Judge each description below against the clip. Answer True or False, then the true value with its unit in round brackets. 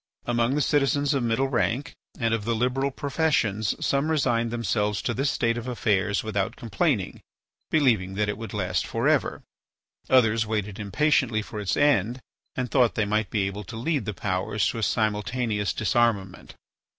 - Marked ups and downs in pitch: False (3.6 semitones)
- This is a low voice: True (115 Hz)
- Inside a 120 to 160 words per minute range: False (170 wpm)